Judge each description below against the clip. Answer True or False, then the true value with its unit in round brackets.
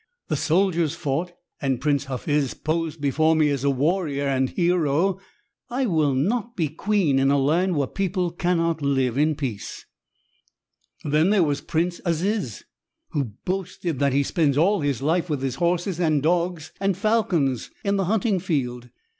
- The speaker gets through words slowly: False (165 wpm)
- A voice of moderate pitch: True (160 Hz)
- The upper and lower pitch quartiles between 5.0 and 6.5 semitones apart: False (4.4 semitones)